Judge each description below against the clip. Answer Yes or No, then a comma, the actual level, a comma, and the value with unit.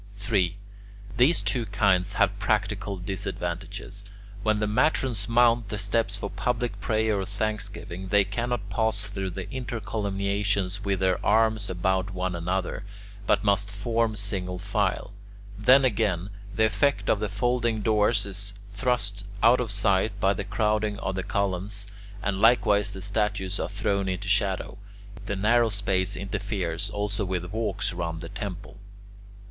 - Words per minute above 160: No, average, 145 wpm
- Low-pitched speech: Yes, low, 100 Hz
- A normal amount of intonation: No, narrow, 2.1 semitones